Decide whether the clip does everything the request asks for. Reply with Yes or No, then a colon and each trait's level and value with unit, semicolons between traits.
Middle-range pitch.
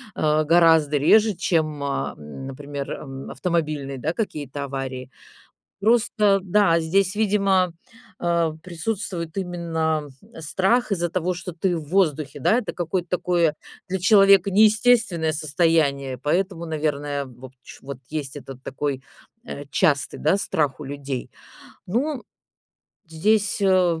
Yes: medium, 165 Hz